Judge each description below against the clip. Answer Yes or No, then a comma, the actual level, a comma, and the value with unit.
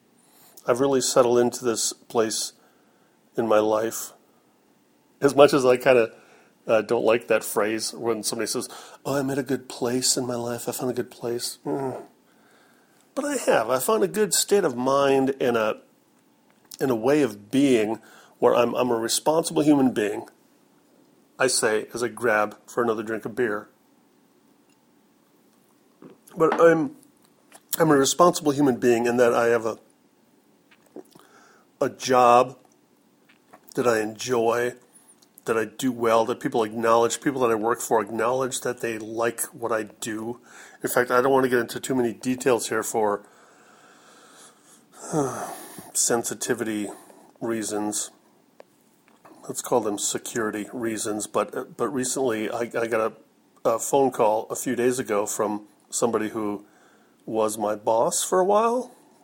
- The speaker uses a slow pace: No, average, 155 wpm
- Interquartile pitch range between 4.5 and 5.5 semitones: No, average, 3.3 semitones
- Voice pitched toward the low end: Yes, low, 120 Hz